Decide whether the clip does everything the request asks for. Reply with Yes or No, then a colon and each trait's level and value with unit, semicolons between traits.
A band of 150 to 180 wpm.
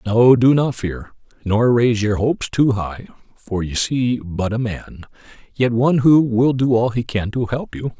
No: average, 195 wpm